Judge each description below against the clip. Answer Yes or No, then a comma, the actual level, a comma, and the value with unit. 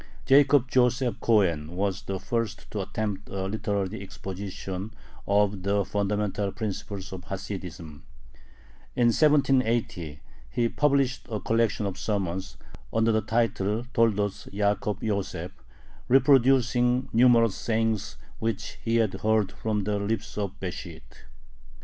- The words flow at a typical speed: No, slow, 120 wpm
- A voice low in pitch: Yes, low, 105 Hz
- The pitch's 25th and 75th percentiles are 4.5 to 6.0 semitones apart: No, average, 3.0 semitones